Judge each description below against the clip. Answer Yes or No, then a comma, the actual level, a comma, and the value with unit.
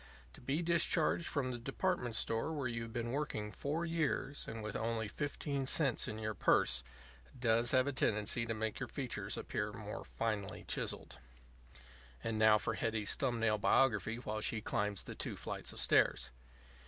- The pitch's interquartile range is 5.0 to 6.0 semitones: No, average, 4.2 semitones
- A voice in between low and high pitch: No, low, 115 Hz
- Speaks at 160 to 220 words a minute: Yes, average, 175 wpm